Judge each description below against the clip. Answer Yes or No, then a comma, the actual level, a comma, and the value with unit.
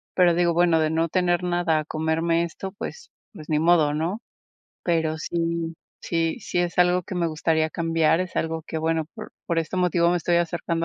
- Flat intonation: Yes, narrow, 1.6 semitones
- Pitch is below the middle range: No, medium, 170 Hz